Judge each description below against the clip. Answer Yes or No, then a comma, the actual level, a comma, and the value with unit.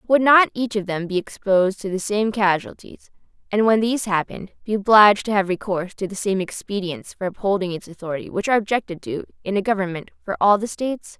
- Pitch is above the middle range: Yes, high, 200 Hz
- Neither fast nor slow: No, fast, 210 wpm